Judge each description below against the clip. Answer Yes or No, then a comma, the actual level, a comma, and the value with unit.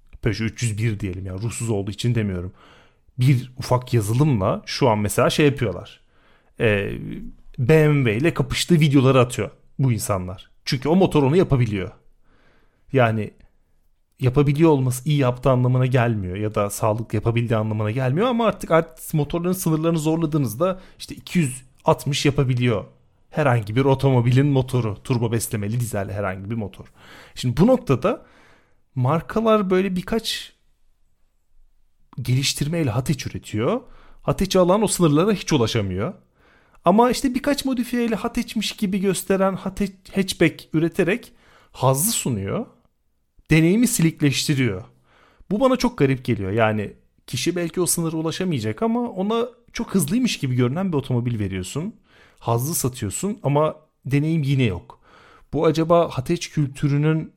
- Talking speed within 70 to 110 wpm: No, average, 125 wpm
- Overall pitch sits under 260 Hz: Yes, medium, 140 Hz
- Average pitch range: No, wide, 6.7 semitones